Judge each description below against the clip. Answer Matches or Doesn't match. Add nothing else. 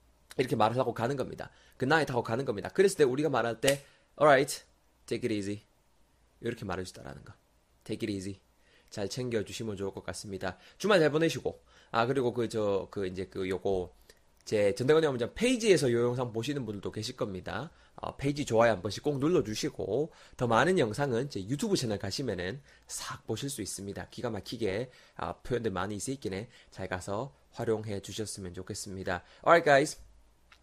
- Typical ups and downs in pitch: Matches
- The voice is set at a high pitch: Doesn't match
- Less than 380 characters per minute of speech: Doesn't match